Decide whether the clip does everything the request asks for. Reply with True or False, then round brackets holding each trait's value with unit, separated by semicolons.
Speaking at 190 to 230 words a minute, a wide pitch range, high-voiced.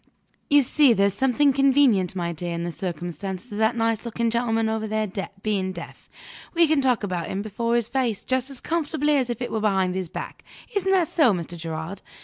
True (205 wpm; 5.7 semitones; 220 Hz)